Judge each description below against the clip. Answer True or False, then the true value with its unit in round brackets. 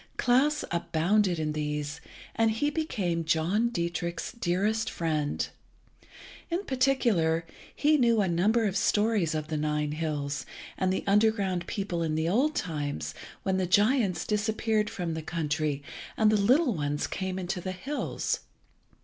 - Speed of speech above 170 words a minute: False (145 wpm)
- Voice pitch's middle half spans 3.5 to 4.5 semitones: False (5.5 semitones)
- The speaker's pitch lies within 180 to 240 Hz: True (185 Hz)